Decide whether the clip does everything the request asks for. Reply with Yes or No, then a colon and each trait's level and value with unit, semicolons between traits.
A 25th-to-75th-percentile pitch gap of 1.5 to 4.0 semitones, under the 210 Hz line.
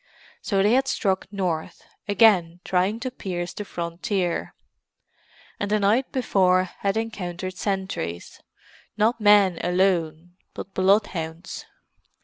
Yes: average, 2.9 semitones; high, 190 Hz